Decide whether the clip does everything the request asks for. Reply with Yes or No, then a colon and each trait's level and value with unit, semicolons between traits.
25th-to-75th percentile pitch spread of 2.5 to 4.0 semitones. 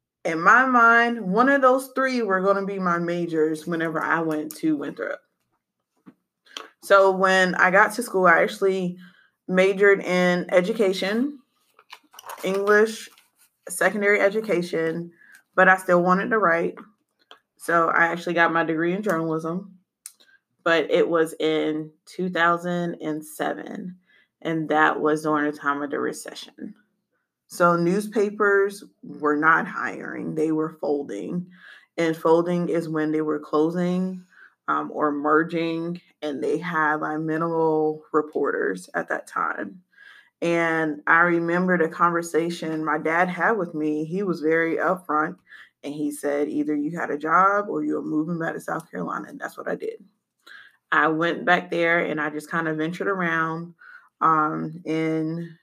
Yes: average, 3.4 semitones